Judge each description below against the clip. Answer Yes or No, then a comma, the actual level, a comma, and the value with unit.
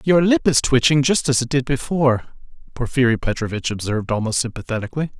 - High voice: No, low, 130 Hz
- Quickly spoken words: No, average, 160 wpm